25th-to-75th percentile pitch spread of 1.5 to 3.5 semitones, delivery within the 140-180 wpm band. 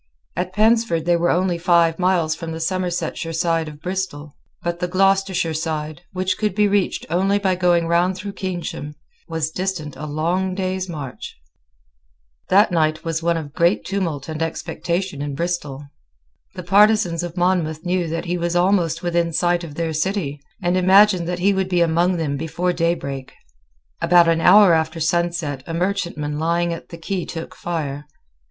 Yes: narrow, 2.4 semitones; average, 170 wpm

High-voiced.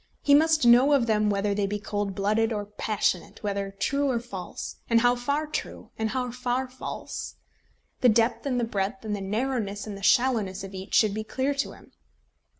Yes: high, 225 Hz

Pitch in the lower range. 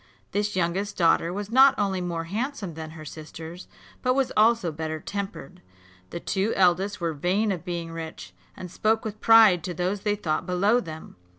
No: medium, 185 Hz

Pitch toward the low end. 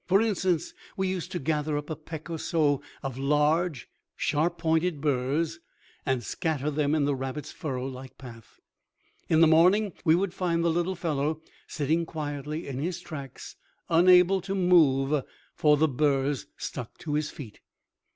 No: medium, 155 Hz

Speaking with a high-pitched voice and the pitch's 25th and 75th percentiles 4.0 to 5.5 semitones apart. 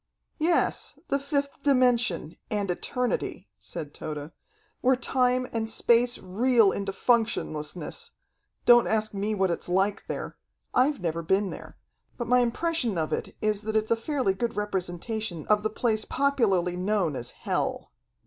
Yes: high, 215 Hz; average, 4.7 semitones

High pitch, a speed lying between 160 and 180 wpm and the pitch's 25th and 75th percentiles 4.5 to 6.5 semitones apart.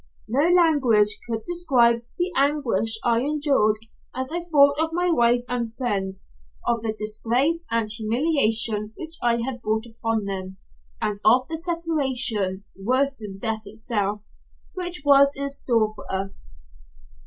No: high, 235 Hz; average, 145 wpm; average, 5.0 semitones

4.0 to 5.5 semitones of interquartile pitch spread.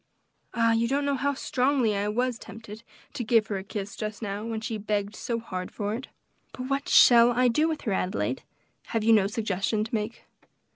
No: average, 2.7 semitones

